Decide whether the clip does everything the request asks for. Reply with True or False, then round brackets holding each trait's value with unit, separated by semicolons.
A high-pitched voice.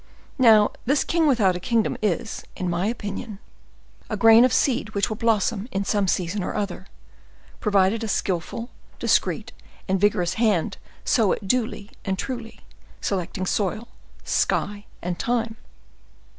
True (210 Hz)